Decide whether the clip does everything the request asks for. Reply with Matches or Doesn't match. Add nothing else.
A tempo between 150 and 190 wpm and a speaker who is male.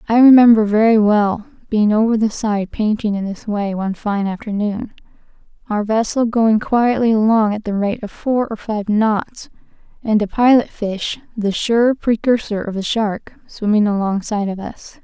Doesn't match